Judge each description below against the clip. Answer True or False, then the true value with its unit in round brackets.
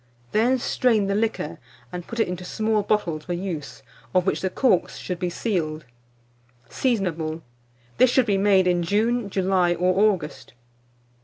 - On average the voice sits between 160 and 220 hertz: True (190 Hz)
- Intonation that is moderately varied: True (3.7 semitones)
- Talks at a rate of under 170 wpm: True (155 wpm)